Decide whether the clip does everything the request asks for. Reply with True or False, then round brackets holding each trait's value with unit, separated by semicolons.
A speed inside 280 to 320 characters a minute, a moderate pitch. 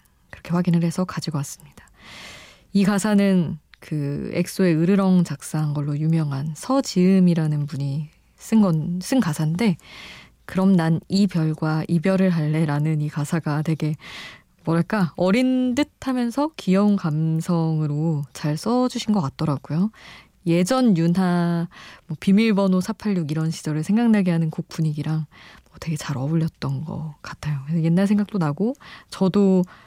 True (285 characters per minute; 170 Hz)